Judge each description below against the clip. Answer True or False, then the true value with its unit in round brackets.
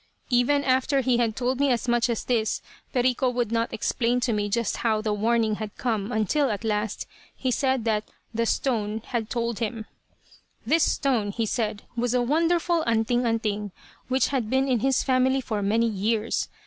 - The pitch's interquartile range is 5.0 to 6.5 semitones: False (2.9 semitones)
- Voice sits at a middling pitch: False (235 Hz)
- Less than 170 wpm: False (185 wpm)